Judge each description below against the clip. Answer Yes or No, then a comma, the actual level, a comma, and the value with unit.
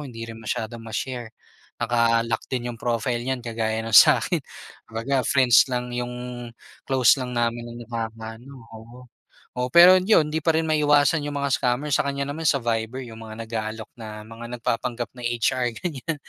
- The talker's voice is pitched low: Yes, low, 120 Hz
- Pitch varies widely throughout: No, average, 2.9 semitones